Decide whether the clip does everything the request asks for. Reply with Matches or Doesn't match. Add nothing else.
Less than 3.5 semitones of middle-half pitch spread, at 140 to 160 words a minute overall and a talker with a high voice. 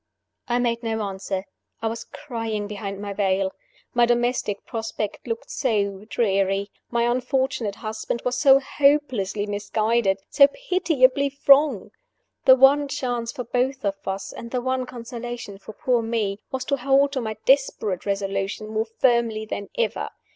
Doesn't match